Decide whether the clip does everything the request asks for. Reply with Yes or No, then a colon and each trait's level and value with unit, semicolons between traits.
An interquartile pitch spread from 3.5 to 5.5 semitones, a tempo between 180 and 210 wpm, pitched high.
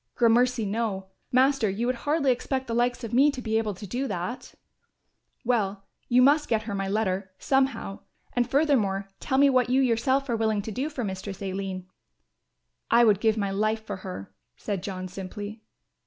Yes: average, 4.4 semitones; average, 185 wpm; high, 225 Hz